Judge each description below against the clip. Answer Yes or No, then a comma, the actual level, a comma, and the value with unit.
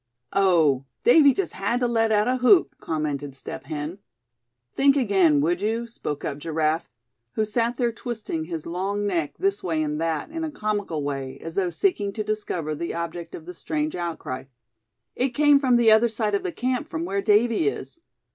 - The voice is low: No, high, 195 Hz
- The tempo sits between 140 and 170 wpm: No, average, 190 wpm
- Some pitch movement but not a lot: No, wide, 6.7 semitones